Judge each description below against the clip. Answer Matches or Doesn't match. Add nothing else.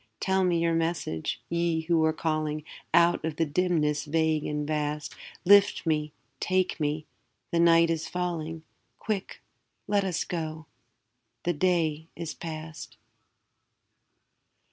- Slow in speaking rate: Matches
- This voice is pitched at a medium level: Matches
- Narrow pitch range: Matches